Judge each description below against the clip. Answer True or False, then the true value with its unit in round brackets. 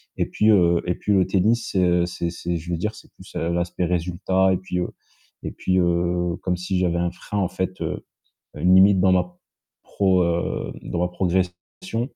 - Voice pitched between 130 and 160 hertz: False (90 Hz)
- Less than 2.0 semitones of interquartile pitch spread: True (1.4 semitones)